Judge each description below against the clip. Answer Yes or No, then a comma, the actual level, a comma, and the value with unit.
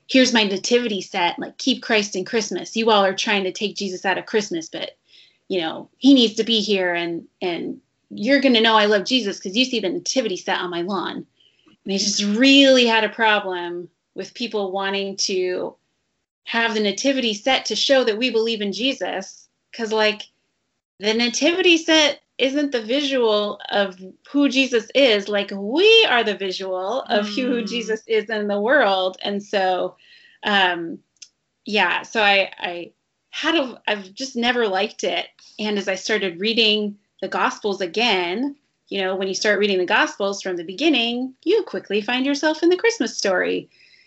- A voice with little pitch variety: No, average, 4.9 semitones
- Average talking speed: Yes, average, 180 wpm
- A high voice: Yes, high, 215 Hz